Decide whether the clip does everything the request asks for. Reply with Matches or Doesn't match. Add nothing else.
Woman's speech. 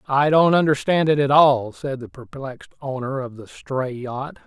Doesn't match